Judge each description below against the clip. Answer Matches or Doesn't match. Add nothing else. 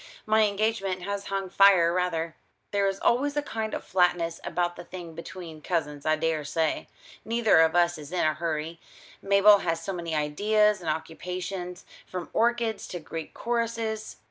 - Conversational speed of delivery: Matches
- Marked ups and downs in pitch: Doesn't match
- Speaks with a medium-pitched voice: Matches